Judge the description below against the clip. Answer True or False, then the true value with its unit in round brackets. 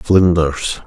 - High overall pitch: False (85 Hz)